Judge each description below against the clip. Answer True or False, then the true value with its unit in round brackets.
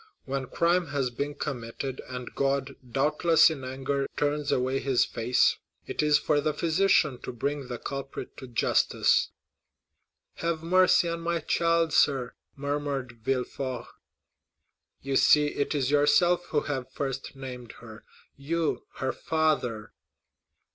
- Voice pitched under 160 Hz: True (140 Hz)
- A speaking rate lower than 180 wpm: True (135 wpm)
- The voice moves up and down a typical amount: True (3.0 semitones)